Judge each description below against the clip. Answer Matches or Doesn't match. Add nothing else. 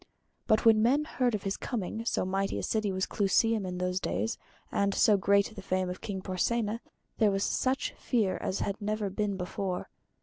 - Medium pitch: Doesn't match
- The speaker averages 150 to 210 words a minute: Matches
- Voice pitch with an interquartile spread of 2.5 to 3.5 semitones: Matches